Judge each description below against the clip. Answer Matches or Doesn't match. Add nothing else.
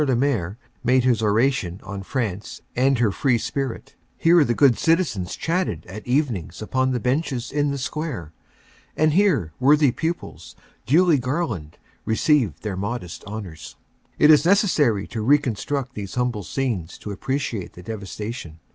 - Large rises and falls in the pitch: Matches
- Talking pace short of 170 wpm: Matches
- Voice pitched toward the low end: Matches